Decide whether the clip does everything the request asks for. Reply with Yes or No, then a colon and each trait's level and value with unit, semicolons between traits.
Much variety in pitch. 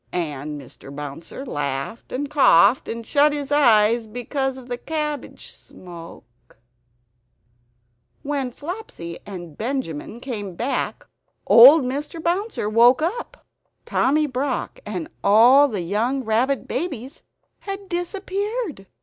Yes: wide, 6.5 semitones